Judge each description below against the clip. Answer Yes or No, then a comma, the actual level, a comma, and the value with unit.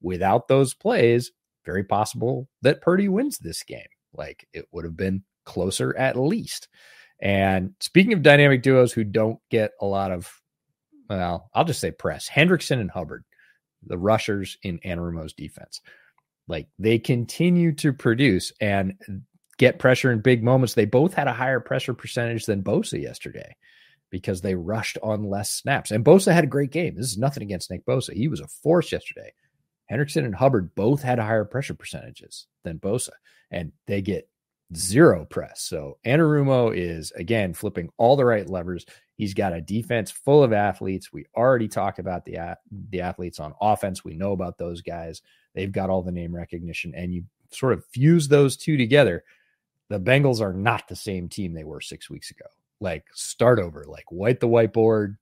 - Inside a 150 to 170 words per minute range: No, average, 180 wpm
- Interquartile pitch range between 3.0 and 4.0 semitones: No, wide, 5.6 semitones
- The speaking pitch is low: Yes, low, 110 Hz